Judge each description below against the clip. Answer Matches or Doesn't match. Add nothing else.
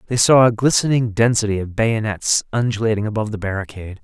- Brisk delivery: Doesn't match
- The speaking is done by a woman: Doesn't match